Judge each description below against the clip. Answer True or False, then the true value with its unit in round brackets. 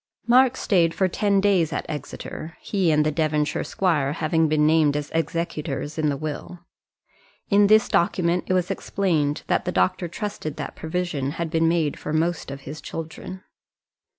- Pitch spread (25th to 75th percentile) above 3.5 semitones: False (3.1 semitones)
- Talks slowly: False (170 wpm)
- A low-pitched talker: False (165 Hz)